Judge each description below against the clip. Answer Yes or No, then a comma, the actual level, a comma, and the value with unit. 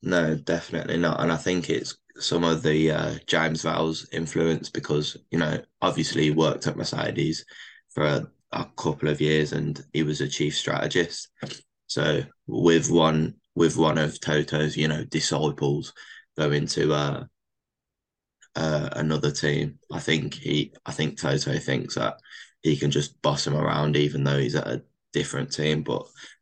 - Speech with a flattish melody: Yes, narrow, 1.3 semitones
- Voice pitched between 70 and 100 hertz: Yes, very low, 75 Hz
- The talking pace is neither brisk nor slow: Yes, average, 165 wpm